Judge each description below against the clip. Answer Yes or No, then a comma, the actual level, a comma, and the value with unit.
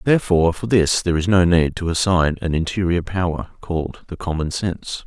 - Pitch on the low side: Yes, very low, 90 Hz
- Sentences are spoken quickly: No, average, 190 wpm